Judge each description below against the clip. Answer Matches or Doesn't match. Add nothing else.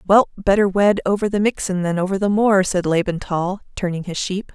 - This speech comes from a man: Doesn't match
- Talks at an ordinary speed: Doesn't match